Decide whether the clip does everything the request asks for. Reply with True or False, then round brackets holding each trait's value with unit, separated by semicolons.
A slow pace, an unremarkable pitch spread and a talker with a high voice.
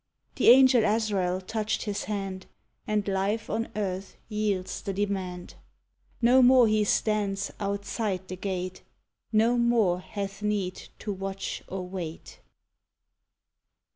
False (120 wpm; 2.2 semitones; 200 Hz)